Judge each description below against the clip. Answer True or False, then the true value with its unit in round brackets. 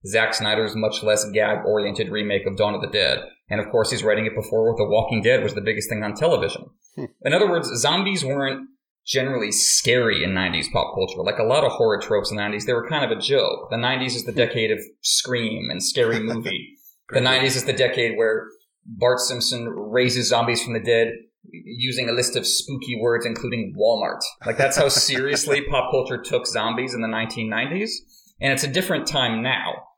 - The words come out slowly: False (200 wpm)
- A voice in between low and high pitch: False (125 Hz)